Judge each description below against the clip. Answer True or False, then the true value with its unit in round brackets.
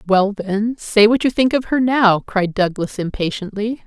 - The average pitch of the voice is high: True (215 Hz)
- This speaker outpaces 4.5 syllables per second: False (4.4 syllables/s)